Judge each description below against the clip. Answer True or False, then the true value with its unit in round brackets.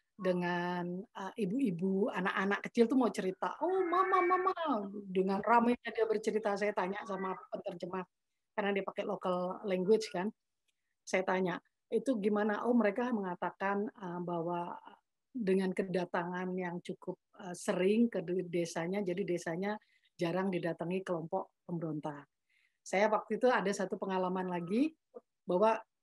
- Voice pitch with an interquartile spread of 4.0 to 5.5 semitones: False (3.1 semitones)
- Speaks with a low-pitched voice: False (195 Hz)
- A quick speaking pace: False (130 wpm)